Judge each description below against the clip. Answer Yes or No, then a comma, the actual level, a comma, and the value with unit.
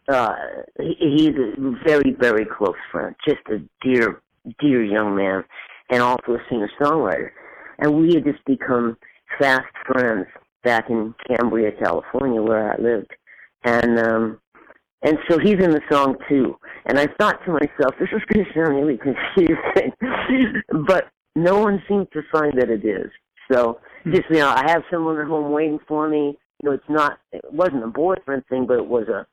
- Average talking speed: Yes, average, 180 wpm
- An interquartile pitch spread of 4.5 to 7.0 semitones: Yes, average, 4.9 semitones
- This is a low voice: No, medium, 145 Hz